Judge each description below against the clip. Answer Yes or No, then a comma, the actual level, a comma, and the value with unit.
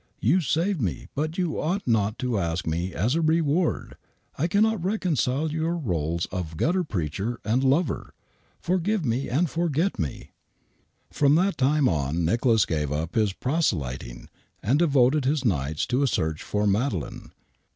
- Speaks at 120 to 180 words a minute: Yes, average, 160 wpm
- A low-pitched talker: Yes, low, 130 Hz